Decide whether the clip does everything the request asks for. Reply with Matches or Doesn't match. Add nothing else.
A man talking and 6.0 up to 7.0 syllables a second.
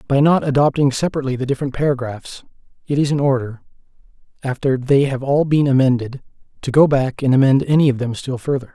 Matches